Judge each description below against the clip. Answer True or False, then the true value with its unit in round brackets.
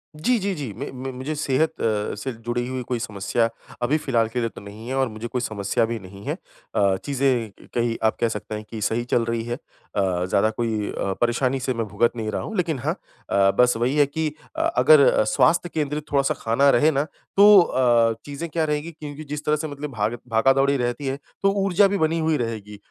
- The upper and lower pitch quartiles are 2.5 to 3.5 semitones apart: False (4.7 semitones)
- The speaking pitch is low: True (125 Hz)